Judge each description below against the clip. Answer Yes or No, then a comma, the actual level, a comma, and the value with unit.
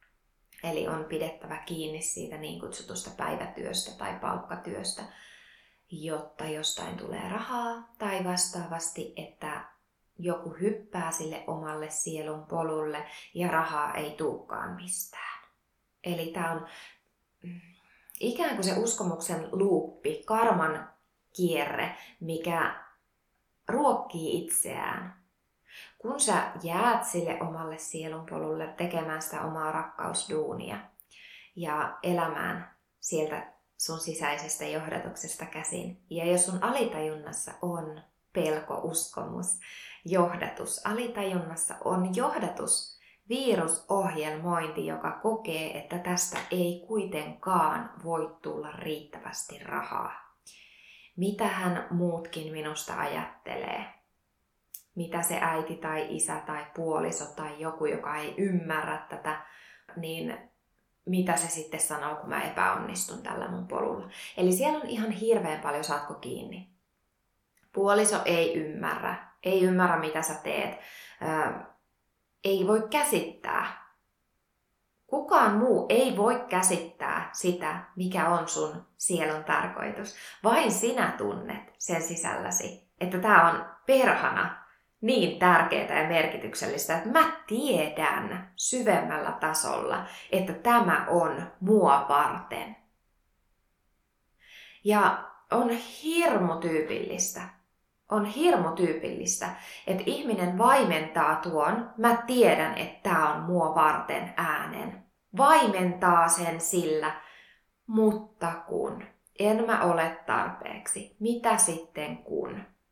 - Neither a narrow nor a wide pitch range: Yes, average, 4.2 semitones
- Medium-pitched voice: Yes, medium, 170 Hz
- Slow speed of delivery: No, average, 105 wpm